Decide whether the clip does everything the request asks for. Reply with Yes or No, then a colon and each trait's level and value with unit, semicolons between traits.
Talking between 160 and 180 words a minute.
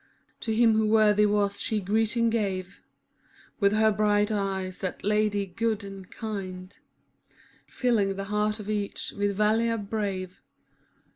No: average, 140 wpm